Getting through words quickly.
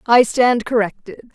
No: slow, 135 wpm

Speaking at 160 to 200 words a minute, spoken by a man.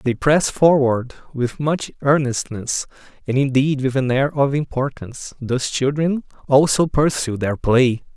No: average, 140 wpm; male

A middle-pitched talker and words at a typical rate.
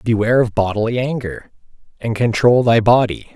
No: low, 115 Hz; average, 145 wpm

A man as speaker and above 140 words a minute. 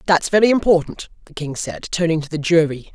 Yes: male; fast, 205 wpm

